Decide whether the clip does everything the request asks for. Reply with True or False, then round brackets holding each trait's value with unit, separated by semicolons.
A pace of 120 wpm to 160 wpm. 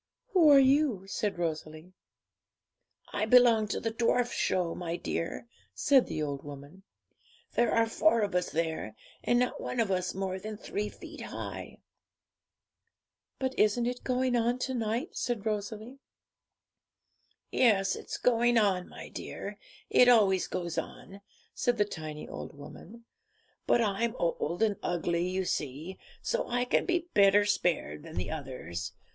True (150 wpm)